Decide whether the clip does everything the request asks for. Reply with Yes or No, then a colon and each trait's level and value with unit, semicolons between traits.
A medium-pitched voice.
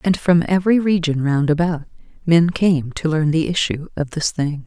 Yes: medium, 165 Hz